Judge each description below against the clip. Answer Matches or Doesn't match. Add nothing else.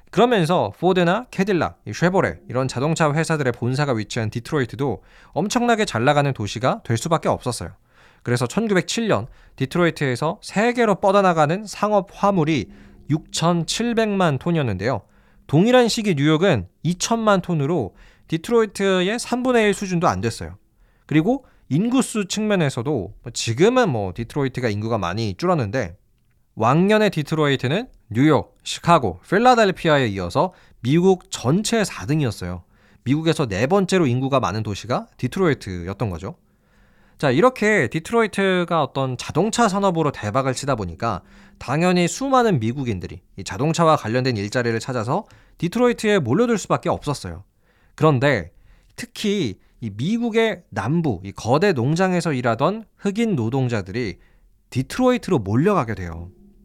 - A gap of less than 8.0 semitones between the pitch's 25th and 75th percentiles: Doesn't match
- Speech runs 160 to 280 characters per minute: Doesn't match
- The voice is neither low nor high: Matches